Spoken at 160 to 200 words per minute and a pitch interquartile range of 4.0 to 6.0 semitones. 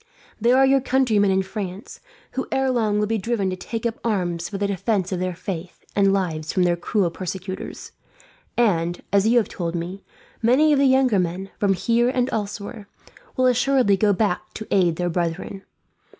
Yes: average, 190 wpm; average, 4.4 semitones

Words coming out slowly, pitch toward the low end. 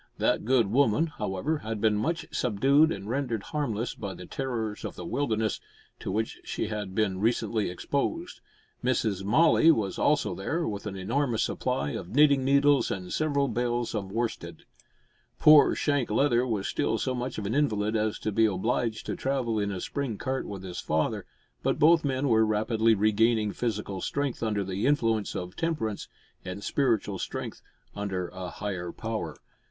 No: average, 170 wpm; low, 110 Hz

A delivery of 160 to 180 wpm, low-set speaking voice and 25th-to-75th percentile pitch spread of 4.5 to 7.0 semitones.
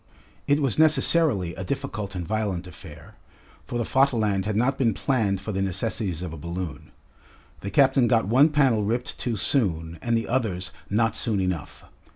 Yes: average, 175 wpm; low, 110 Hz; wide, 5.5 semitones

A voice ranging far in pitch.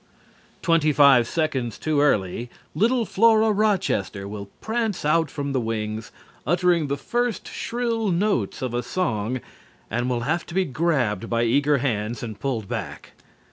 Yes: wide, 7.6 semitones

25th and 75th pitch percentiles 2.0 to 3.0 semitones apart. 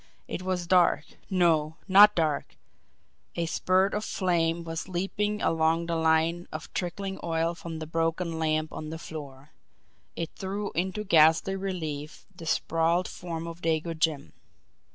Yes: narrow, 2.4 semitones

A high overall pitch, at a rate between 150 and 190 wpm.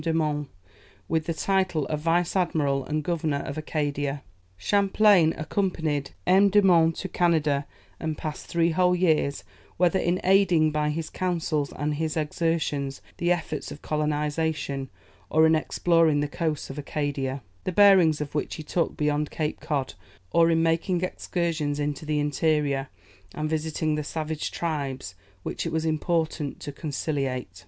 No: medium, 155 Hz; average, 155 wpm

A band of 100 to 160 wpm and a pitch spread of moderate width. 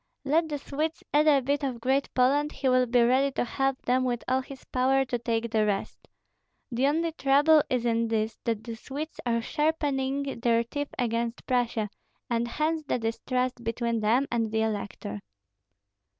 No: average, 180 wpm; average, 3.3 semitones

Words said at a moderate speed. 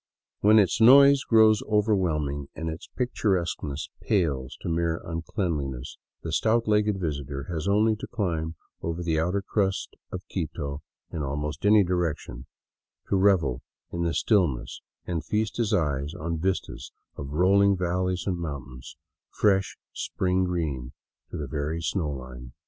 Yes: average, 145 wpm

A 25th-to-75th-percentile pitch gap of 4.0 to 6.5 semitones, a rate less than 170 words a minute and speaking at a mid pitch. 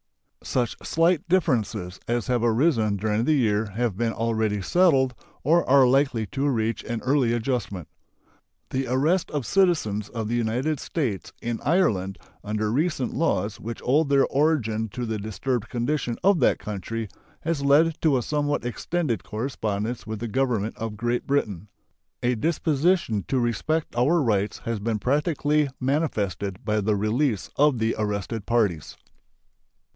No: average, 5.1 semitones; average, 150 wpm; low, 120 Hz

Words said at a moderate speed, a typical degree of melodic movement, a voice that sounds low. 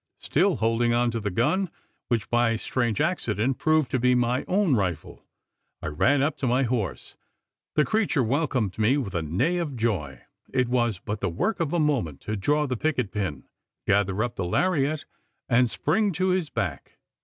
No: average, 190 wpm; wide, 6.2 semitones; low, 120 Hz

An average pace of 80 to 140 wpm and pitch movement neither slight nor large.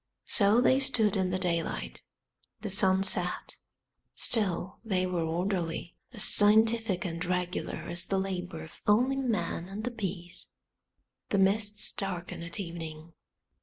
Yes: slow, 135 wpm; average, 3.3 semitones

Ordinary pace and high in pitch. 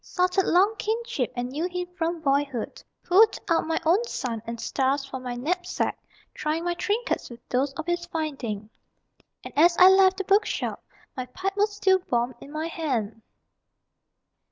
Yes: average, 170 wpm; very high, 325 Hz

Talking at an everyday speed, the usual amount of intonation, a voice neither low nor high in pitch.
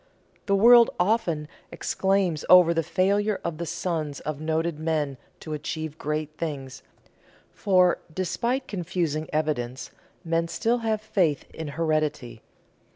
No: slow, 125 wpm; average, 3.6 semitones; medium, 165 Hz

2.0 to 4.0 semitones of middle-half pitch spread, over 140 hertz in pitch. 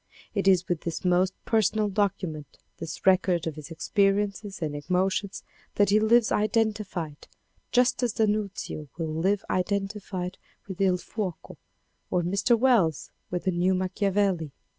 Yes: average, 2.9 semitones; high, 190 Hz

